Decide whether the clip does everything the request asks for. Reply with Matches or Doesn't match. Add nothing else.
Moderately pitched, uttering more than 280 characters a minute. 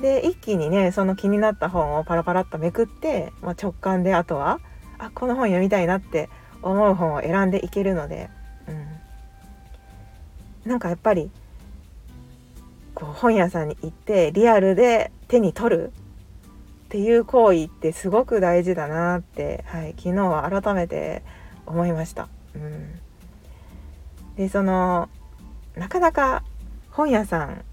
Doesn't match